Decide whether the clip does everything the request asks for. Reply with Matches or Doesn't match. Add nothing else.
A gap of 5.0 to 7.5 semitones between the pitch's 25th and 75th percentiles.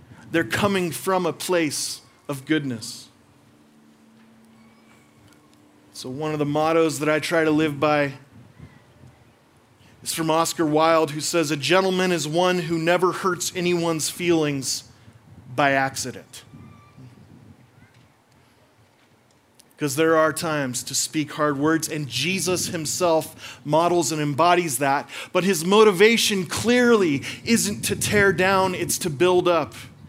Matches